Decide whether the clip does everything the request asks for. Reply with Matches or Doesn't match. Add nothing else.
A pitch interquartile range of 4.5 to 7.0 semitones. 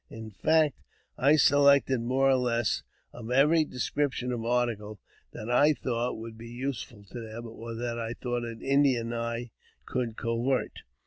Doesn't match